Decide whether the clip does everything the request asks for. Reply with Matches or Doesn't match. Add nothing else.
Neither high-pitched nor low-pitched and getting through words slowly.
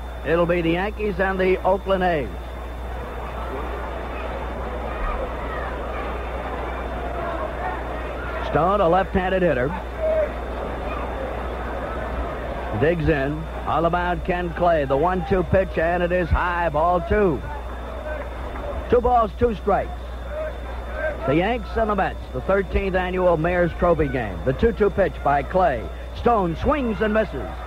Matches